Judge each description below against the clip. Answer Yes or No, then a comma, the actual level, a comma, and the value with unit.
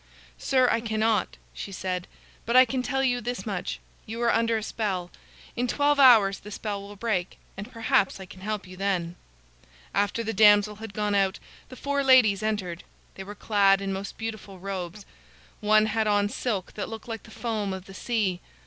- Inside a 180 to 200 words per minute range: Yes, average, 195 wpm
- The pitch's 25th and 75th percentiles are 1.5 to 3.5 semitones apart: Yes, average, 2.7 semitones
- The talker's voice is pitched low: No, high, 210 Hz